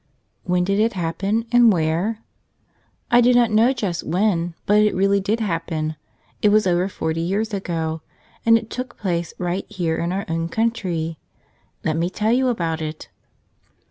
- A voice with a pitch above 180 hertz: Yes, high, 190 Hz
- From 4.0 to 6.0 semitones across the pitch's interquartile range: Yes, average, 4.7 semitones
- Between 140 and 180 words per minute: Yes, average, 170 wpm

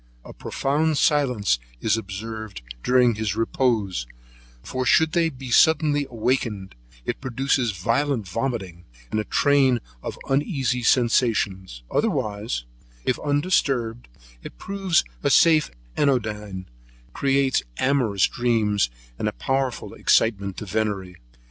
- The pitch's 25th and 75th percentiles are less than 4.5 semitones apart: No, average, 4.8 semitones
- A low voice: Yes, low, 120 Hz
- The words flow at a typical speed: No, slow, 115 wpm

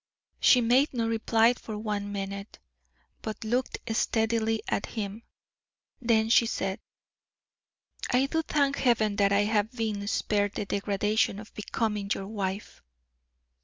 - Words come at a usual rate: No, slow, 130 wpm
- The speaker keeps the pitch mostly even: Yes, narrow, 2.2 semitones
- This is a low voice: No, high, 220 Hz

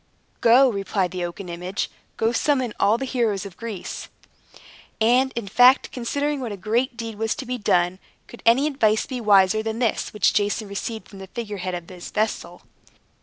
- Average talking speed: Yes, average, 185 wpm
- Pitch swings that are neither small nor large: Yes, average, 3.8 semitones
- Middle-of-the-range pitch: No, high, 220 Hz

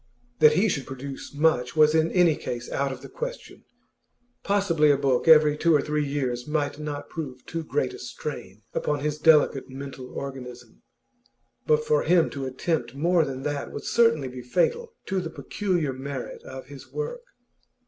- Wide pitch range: No, average, 3.8 semitones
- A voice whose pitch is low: No, medium, 150 Hz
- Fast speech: No, average, 175 wpm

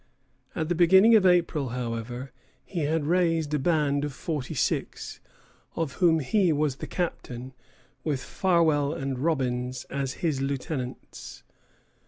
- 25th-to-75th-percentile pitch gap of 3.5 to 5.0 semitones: Yes, average, 4.1 semitones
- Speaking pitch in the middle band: Yes, medium, 150 Hz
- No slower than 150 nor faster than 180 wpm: No, slow, 135 wpm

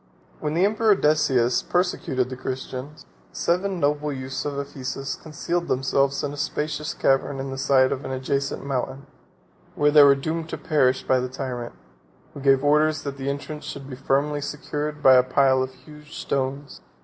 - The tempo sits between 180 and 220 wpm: Yes, average, 185 wpm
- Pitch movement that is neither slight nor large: No, narrow, 2.2 semitones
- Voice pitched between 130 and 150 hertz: Yes, medium, 140 Hz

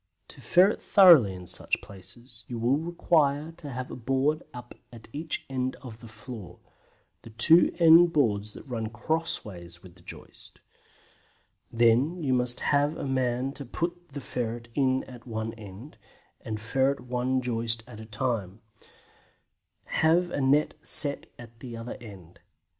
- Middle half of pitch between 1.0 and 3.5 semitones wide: No, average, 4.2 semitones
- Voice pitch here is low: Yes, low, 125 Hz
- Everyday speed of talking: Yes, average, 155 wpm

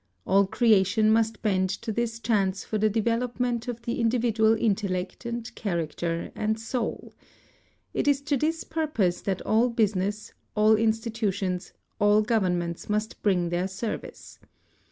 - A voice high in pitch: Yes, high, 215 Hz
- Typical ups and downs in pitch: Yes, average, 3.3 semitones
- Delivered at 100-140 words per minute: Yes, slow, 135 wpm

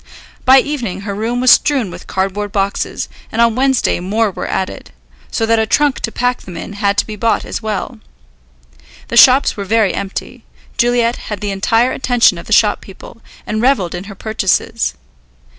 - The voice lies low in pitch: No, high, 220 Hz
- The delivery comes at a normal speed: Yes, average, 185 wpm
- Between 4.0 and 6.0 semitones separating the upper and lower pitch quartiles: No, average, 3.5 semitones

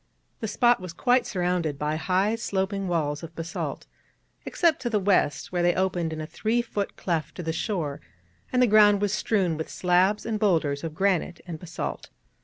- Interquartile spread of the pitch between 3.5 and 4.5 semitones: Yes, average, 4.2 semitones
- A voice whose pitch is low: No, medium, 185 Hz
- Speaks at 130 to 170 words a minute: No, average, 190 wpm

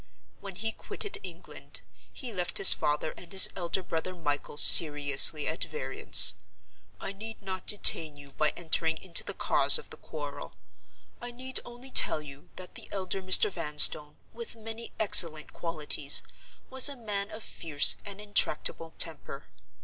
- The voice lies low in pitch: No, medium, 185 Hz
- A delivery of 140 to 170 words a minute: Yes, average, 155 wpm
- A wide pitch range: Yes, wide, 5.9 semitones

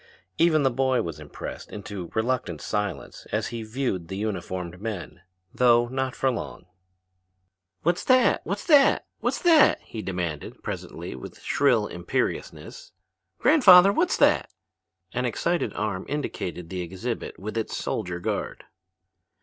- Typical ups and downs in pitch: No, wide, 7.1 semitones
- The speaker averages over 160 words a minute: No, slow, 135 wpm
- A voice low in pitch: Yes, low, 110 Hz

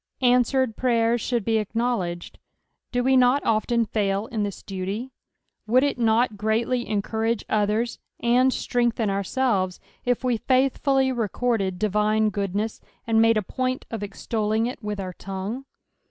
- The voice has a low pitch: No, high, 225 Hz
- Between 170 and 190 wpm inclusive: No, average, 140 wpm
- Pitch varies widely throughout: No, average, 3.0 semitones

